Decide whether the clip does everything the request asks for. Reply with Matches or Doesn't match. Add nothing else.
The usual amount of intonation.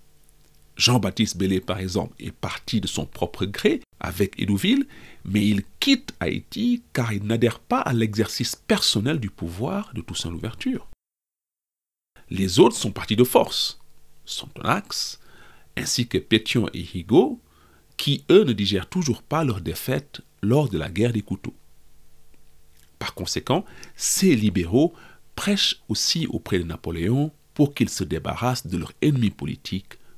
Doesn't match